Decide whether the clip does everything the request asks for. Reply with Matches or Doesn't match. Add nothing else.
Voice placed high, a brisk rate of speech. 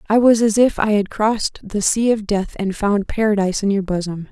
Matches